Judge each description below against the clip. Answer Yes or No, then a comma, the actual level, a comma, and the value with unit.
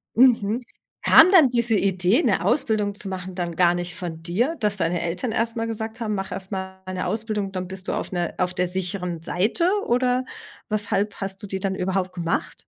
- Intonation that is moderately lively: Yes, average, 3.6 semitones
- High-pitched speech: Yes, high, 195 Hz